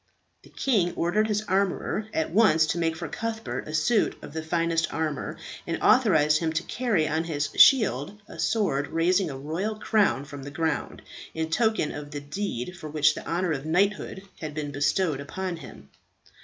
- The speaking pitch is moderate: Yes, medium, 165 Hz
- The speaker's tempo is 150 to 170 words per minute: No, average, 185 wpm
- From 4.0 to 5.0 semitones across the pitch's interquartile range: Yes, average, 4.7 semitones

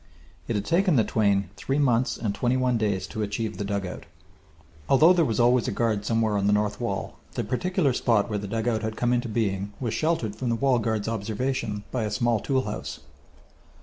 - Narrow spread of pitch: No, average, 3.3 semitones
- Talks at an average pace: No, fast, 210 wpm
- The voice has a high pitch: No, low, 115 Hz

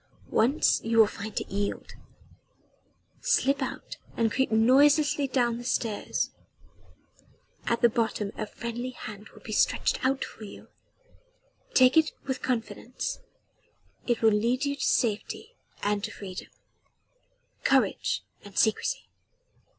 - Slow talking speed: Yes, slow, 125 wpm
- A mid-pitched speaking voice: No, high, 235 Hz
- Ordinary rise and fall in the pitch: Yes, average, 3.5 semitones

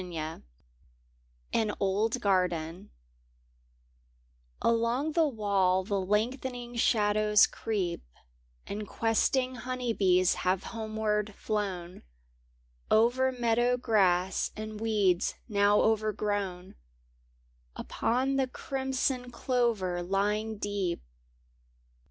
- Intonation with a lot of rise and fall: No, average, 3.9 semitones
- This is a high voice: Yes, high, 215 Hz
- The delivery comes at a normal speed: No, slow, 85 wpm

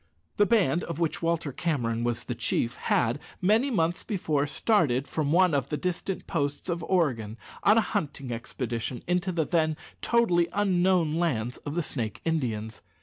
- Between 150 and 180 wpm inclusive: Yes, average, 165 wpm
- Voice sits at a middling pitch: Yes, medium, 160 Hz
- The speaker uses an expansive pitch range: Yes, wide, 6.0 semitones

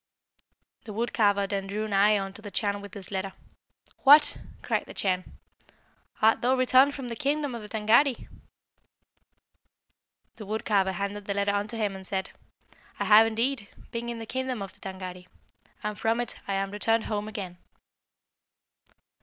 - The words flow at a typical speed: Yes, average, 165 wpm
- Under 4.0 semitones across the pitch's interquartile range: Yes, average, 2.8 semitones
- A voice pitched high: Yes, high, 210 Hz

